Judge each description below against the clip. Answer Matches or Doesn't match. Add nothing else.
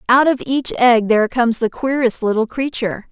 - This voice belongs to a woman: Matches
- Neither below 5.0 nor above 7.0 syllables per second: Matches